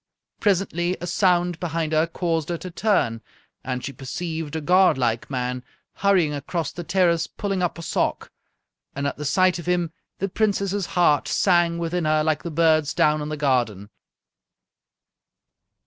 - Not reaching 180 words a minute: Yes, average, 160 wpm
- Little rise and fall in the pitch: No, average, 3.2 semitones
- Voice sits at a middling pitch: Yes, medium, 165 Hz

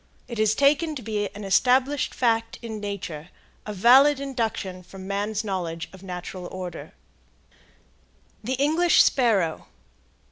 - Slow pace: Yes, slow, 130 wpm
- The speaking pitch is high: Yes, high, 215 Hz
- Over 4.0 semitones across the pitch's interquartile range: Yes, wide, 5.5 semitones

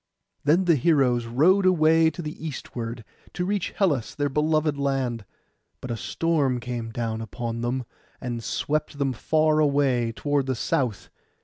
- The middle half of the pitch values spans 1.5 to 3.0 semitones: No, average, 4.5 semitones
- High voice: No, medium, 140 Hz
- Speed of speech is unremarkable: Yes, average, 150 wpm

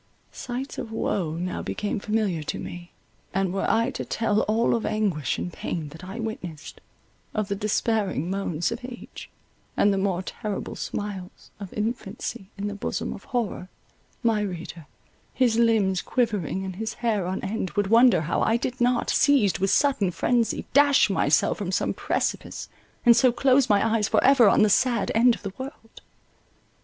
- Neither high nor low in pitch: No, high, 210 Hz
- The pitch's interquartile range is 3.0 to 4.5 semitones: Yes, average, 3.6 semitones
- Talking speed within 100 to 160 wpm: No, average, 175 wpm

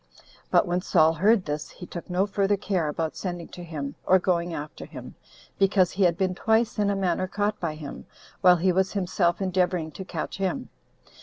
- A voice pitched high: No, medium, 180 Hz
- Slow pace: No, average, 200 wpm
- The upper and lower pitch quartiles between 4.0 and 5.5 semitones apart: No, narrow, 2.4 semitones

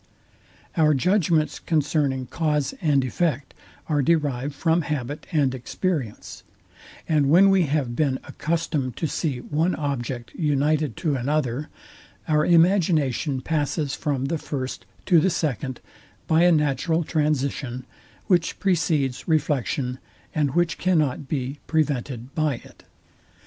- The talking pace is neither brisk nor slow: No, slow, 125 wpm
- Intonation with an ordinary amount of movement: Yes, average, 3.3 semitones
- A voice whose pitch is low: No, medium, 150 Hz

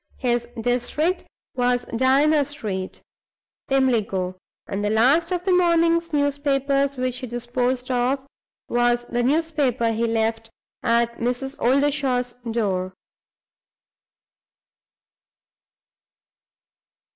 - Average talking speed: No, slow, 90 wpm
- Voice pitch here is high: Yes, very high, 250 Hz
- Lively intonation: No, average, 3.3 semitones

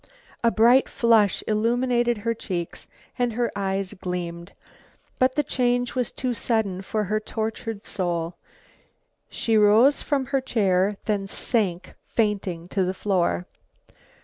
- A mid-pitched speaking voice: No, high, 215 Hz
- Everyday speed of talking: No, slow, 130 wpm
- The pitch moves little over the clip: No, average, 4.1 semitones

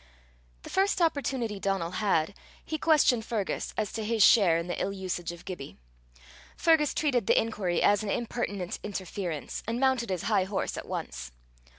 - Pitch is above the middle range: Yes, high, 205 Hz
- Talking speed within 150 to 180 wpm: Yes, average, 170 wpm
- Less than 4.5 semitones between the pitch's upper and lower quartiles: No, average, 4.8 semitones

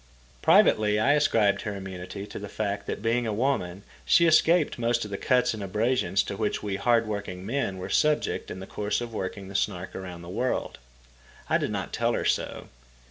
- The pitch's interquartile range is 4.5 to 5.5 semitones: No, average, 3.7 semitones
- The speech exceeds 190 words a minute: Yes, average, 200 wpm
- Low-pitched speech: Yes, low, 105 Hz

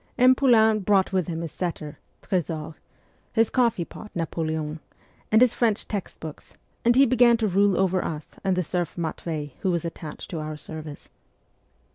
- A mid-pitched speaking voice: Yes, medium, 180 Hz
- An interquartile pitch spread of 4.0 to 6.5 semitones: Yes, wide, 5.5 semitones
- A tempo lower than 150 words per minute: No, average, 170 wpm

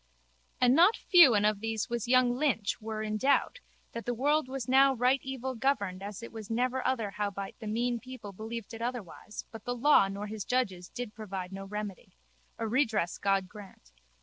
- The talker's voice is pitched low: No, high, 225 Hz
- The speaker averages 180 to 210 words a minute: Yes, average, 195 wpm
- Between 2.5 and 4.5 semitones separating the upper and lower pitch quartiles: Yes, average, 3.7 semitones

